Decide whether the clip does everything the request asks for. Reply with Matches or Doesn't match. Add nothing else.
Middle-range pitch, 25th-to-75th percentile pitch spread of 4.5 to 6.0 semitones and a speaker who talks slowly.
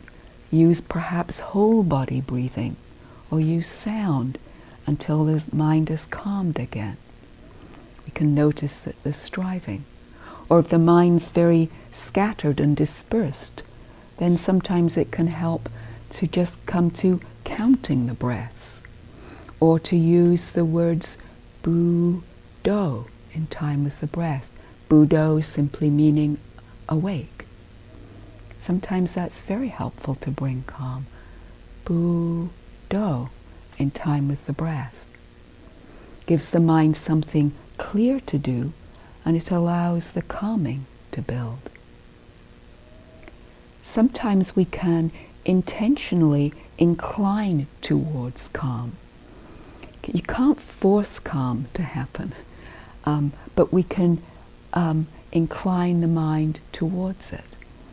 Matches